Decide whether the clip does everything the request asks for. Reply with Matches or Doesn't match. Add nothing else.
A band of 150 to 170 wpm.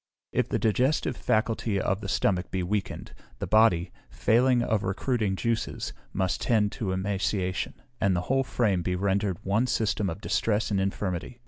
Matches